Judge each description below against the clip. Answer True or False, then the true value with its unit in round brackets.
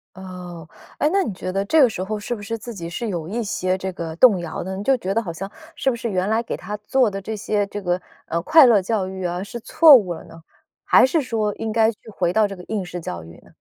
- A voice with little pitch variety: False (3.9 semitones)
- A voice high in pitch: True (200 Hz)